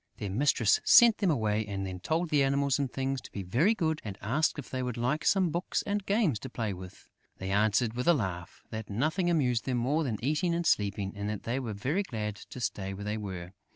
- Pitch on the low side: Yes, low, 125 Hz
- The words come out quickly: Yes, fast, 240 wpm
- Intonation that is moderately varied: No, wide, 6.9 semitones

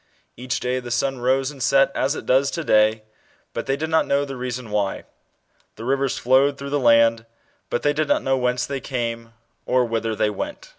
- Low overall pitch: Yes, low, 130 Hz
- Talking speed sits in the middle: No, fast, 210 wpm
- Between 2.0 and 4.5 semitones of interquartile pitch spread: Yes, average, 3.0 semitones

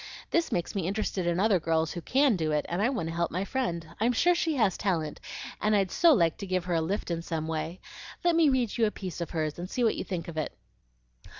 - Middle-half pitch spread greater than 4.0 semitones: Yes, wide, 5.4 semitones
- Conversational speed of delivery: No, fast, 265 wpm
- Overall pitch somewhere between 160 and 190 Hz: Yes, medium, 185 Hz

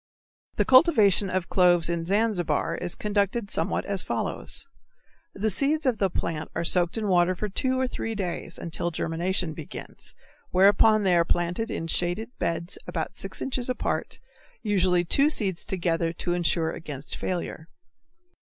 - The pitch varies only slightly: No, average, 3.9 semitones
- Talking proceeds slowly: No, average, 155 wpm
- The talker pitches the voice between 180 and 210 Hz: Yes, medium, 185 Hz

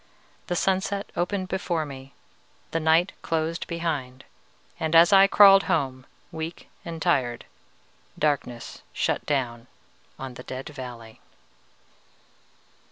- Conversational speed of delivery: No, slow, 110 wpm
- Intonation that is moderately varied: Yes, average, 5.0 semitones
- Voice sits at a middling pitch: Yes, medium, 160 Hz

